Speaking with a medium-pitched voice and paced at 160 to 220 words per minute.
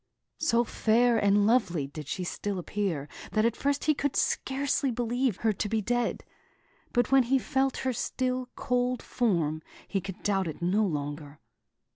No: high, 225 Hz; average, 165 wpm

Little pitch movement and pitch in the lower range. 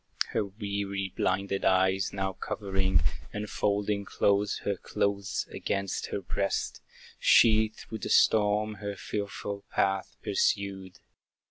Yes: narrow, 1.1 semitones; low, 100 Hz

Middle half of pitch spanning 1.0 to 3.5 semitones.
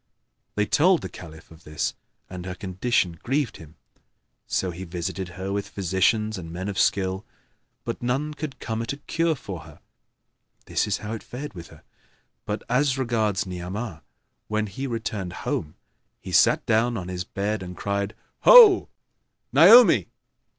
No: average, 4.8 semitones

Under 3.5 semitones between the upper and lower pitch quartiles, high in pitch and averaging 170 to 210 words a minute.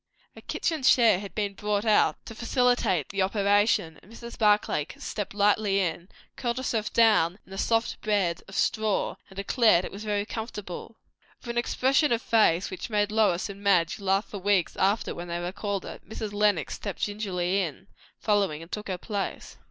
Yes: narrow, 2.5 semitones; high, 205 Hz; average, 185 wpm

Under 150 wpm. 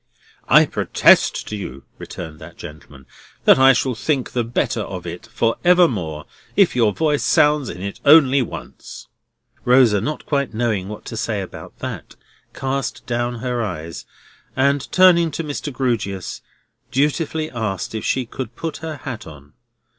No: average, 155 wpm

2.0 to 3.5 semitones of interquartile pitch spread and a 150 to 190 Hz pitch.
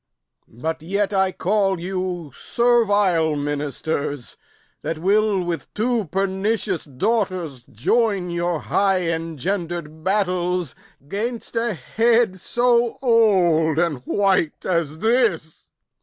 No: average, 4.5 semitones; medium, 185 Hz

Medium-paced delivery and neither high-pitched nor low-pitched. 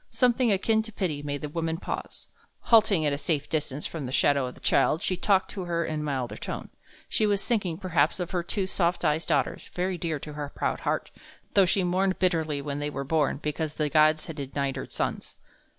No: fast, 220 wpm; medium, 160 Hz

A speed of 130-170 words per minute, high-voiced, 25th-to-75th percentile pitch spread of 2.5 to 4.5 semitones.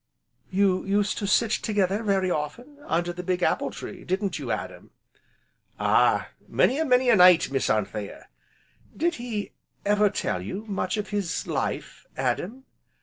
Yes: average, 150 wpm; high, 200 Hz; average, 3.5 semitones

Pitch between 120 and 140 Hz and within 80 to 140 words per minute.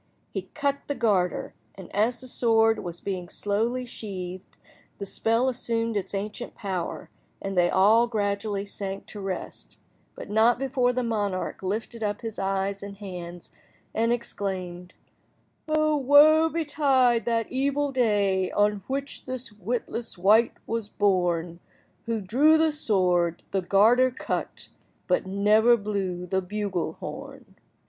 No: high, 210 Hz; slow, 135 wpm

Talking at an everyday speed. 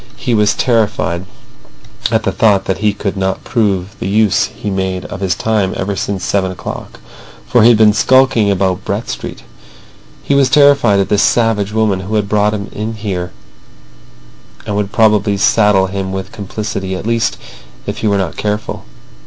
Yes: average, 180 wpm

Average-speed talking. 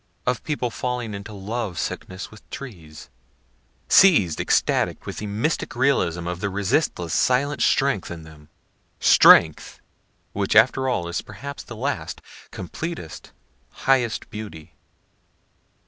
No: slow, 120 wpm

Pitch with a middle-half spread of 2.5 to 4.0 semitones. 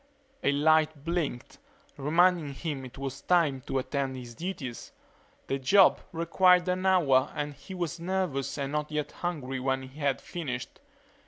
No: average, 4.4 semitones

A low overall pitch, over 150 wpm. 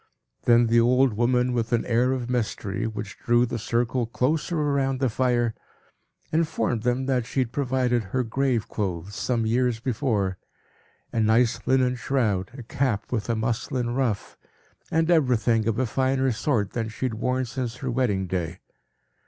Yes: low, 120 Hz; average, 160 wpm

